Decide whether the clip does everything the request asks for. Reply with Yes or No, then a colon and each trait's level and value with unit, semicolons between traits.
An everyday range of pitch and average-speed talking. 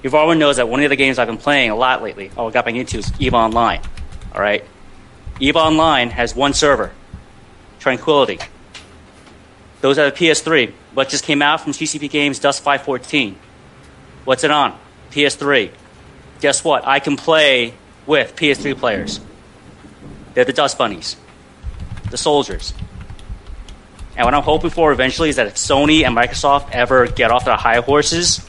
Yes: average, 3.8 semitones; average, 165 wpm